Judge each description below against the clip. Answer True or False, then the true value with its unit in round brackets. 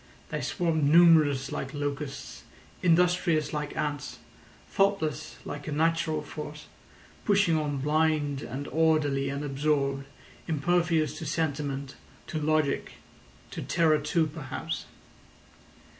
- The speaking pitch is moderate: True (150 Hz)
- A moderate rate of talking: False (110 wpm)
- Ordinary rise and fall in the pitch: False (2.1 semitones)